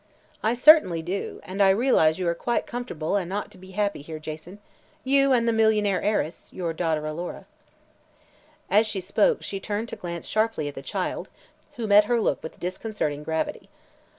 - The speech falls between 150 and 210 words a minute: Yes, average, 180 wpm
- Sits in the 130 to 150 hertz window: No, high, 195 Hz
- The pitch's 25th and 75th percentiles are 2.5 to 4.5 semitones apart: No, average, 4.9 semitones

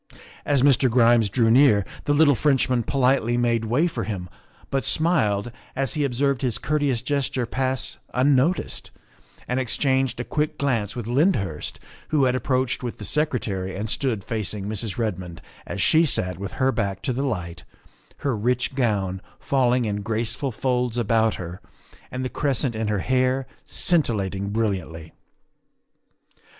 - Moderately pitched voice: No, low, 120 Hz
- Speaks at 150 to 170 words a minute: Yes, average, 165 wpm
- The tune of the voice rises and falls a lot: No, average, 4.2 semitones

